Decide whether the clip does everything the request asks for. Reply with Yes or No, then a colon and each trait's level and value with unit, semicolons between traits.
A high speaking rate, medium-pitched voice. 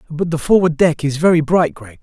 Yes: fast, 240 wpm; medium, 160 Hz